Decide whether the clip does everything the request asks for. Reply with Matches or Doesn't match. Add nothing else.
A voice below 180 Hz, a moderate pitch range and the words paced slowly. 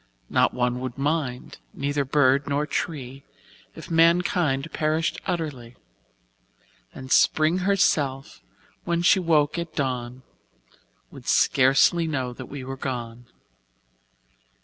Matches